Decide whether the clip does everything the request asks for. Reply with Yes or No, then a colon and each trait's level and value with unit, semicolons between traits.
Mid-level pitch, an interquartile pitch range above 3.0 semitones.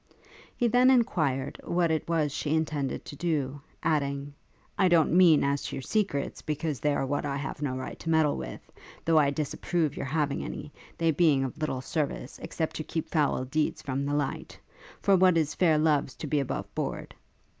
No: medium, 150 Hz; average, 2.7 semitones